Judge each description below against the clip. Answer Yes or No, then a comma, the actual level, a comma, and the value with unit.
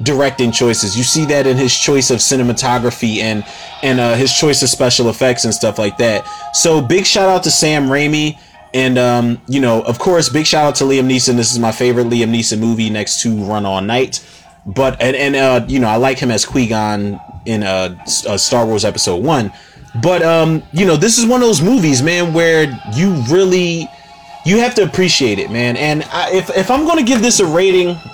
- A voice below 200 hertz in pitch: Yes, low, 135 Hz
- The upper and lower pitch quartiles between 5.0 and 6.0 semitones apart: Yes, wide, 5.6 semitones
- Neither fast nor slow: No, fast, 215 wpm